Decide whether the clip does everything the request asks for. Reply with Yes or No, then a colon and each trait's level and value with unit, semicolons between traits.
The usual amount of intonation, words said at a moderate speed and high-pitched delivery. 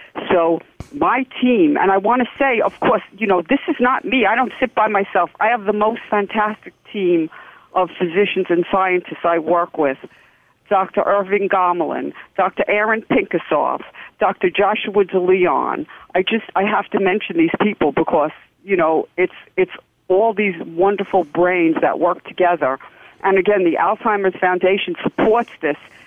Yes: average, 3.3 semitones; average, 160 wpm; high, 195 Hz